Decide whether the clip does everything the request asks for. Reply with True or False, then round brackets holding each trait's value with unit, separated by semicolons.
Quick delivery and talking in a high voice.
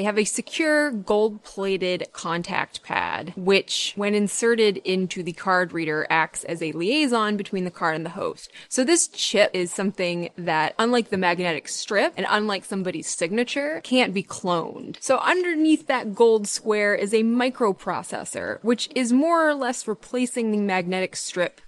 False (165 wpm; 205 Hz)